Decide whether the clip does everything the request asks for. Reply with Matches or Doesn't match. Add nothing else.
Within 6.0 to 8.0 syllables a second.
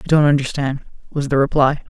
Matches